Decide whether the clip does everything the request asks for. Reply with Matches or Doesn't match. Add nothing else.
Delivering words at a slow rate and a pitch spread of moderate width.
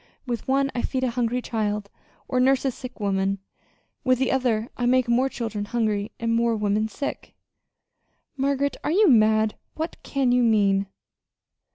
Doesn't match